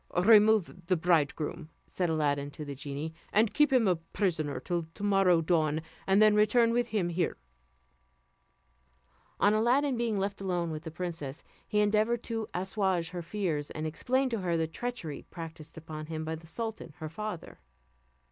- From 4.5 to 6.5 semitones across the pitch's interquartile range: Yes, average, 5.0 semitones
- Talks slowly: No, average, 165 wpm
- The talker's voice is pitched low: No, medium, 180 Hz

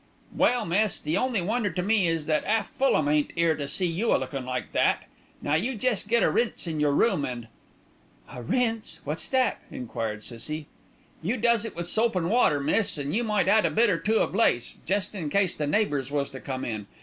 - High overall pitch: No, medium, 175 Hz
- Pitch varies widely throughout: Yes, wide, 7.2 semitones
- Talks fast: Yes, fast, 225 wpm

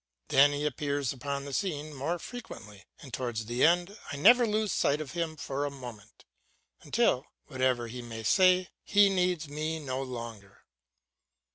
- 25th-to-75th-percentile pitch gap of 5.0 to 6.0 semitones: Yes, wide, 5.5 semitones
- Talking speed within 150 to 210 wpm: Yes, average, 160 wpm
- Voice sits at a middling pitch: Yes, medium, 145 Hz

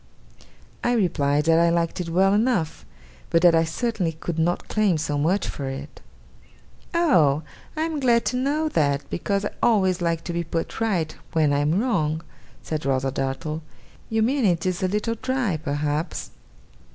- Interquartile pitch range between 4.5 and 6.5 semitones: Yes, wide, 5.6 semitones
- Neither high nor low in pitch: Yes, medium, 170 Hz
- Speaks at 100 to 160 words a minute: No, average, 175 wpm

